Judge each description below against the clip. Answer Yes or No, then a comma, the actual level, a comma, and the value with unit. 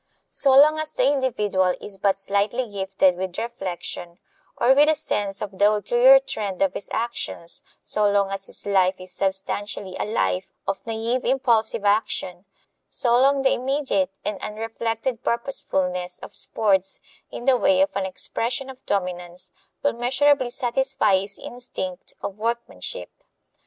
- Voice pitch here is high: Yes, high, 210 Hz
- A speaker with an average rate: Yes, average, 150 wpm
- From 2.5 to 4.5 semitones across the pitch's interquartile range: No, average, 5.0 semitones